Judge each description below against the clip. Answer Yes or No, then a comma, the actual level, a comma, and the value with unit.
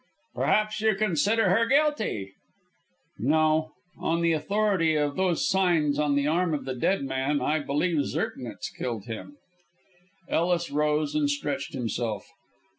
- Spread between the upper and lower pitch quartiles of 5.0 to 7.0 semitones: Yes, average, 5.3 semitones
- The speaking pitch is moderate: Yes, medium, 155 Hz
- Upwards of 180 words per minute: No, slow, 135 wpm